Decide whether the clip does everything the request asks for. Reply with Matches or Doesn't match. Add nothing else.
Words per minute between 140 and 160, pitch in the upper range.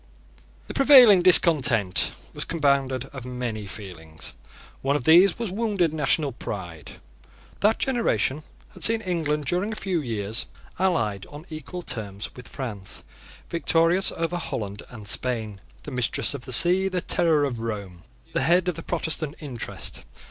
Doesn't match